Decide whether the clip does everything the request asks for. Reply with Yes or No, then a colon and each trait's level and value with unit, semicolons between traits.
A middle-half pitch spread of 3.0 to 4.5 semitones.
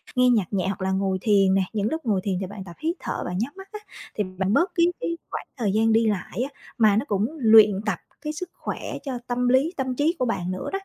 No: average, 5.3 semitones